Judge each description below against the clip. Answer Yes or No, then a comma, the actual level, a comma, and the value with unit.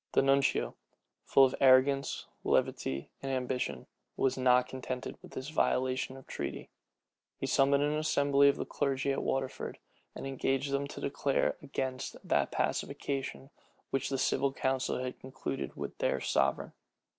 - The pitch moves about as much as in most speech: No, narrow, 1.2 semitones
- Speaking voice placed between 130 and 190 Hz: Yes, low, 135 Hz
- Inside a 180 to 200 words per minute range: No, average, 145 wpm